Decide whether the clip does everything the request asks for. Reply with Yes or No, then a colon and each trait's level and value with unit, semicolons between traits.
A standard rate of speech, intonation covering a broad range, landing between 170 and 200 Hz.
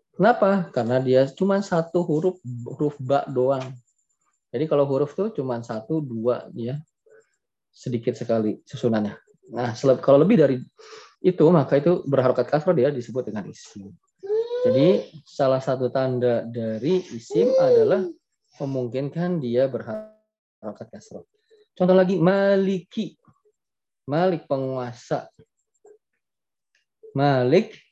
No: average, 105 wpm; wide, 7.5 semitones; medium, 150 Hz